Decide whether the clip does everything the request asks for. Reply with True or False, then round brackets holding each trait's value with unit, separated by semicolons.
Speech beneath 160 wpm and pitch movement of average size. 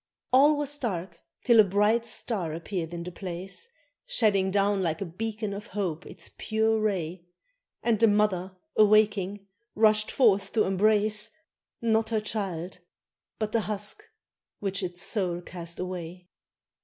True (145 wpm; 3.1 semitones)